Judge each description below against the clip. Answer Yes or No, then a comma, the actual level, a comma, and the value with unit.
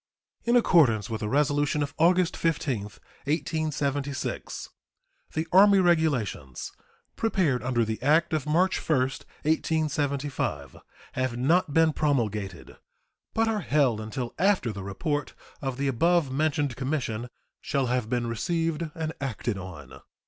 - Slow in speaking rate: Yes, slow, 125 wpm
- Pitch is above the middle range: No, medium, 140 Hz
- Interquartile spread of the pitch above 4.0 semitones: Yes, average, 5.1 semitones